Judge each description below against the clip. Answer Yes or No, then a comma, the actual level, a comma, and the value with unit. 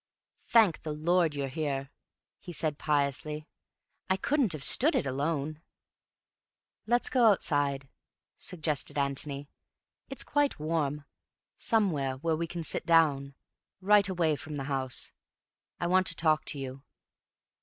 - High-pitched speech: No, medium, 155 Hz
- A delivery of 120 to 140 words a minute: Yes, slow, 135 wpm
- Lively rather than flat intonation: No, average, 4.1 semitones